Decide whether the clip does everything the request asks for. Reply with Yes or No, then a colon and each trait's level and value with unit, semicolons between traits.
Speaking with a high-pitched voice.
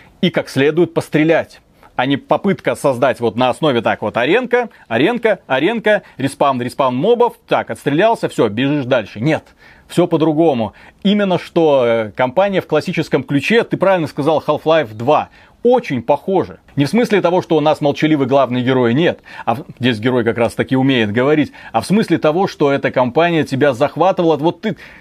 No: medium, 155 Hz